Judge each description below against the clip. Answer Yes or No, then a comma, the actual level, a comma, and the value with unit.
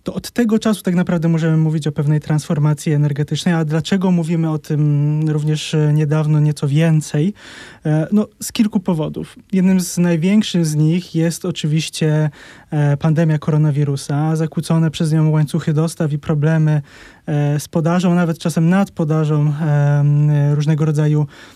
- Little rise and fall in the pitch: Yes, narrow, 2.1 semitones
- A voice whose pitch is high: No, medium, 155 Hz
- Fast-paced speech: No, average, 135 wpm